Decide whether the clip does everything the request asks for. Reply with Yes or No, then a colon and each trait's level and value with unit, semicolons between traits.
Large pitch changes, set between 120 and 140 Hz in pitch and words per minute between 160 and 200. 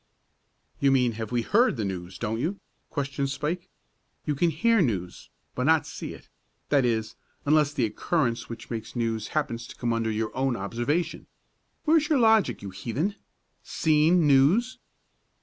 Yes: wide, 6.0 semitones; low, 135 Hz; average, 165 wpm